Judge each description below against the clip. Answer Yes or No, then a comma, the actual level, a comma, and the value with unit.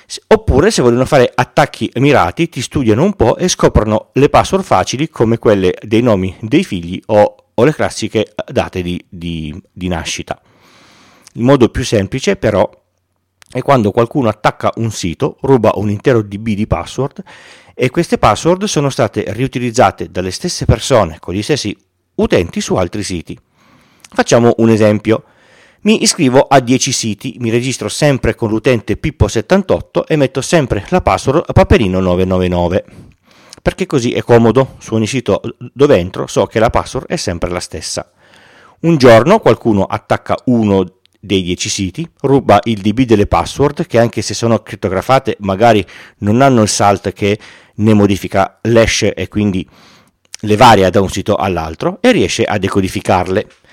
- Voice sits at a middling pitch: No, low, 110 Hz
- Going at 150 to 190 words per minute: Yes, average, 155 wpm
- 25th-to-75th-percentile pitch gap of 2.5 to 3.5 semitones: No, average, 5.3 semitones